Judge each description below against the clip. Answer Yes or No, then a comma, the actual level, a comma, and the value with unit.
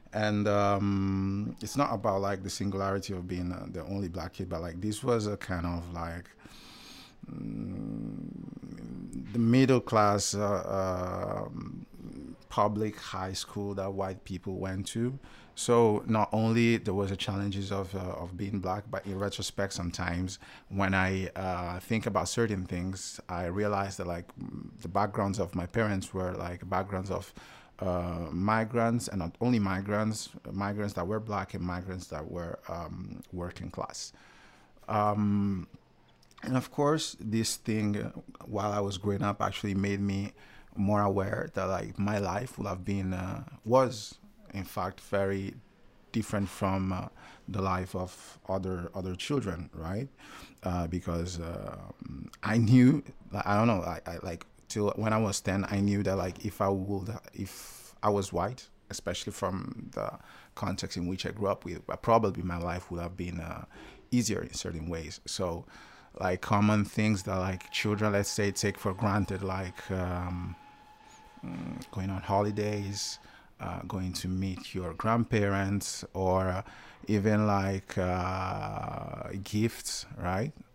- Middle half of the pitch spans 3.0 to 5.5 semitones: No, narrow, 2.4 semitones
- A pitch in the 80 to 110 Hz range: Yes, low, 100 Hz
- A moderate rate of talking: Yes, average, 150 wpm